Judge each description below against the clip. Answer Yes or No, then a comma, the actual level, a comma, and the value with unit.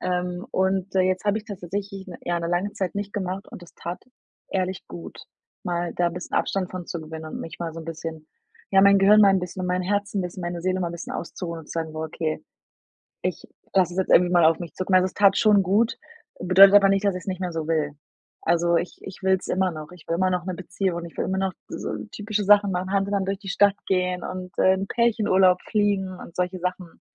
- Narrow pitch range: Yes, narrow, 2.1 semitones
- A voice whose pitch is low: No, medium, 185 Hz